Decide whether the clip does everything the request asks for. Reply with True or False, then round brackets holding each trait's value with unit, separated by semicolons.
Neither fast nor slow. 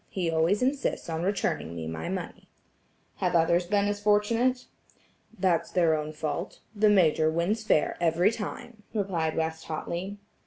True (150 wpm)